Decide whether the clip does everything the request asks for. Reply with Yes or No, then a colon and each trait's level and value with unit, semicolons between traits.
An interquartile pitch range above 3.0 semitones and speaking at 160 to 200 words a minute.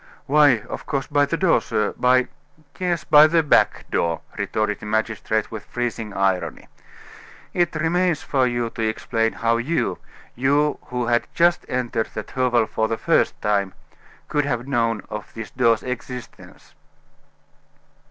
No: average, 4.7 semitones; average, 150 wpm